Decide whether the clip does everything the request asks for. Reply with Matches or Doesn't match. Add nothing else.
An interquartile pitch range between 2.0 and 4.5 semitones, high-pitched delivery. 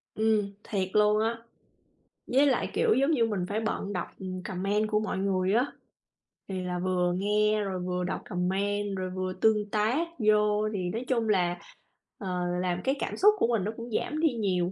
Matches